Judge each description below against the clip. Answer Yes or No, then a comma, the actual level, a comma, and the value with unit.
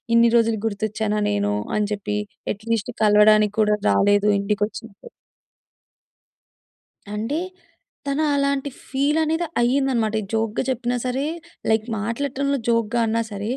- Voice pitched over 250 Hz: No, high, 225 Hz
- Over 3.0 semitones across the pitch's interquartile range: Yes, average, 4.0 semitones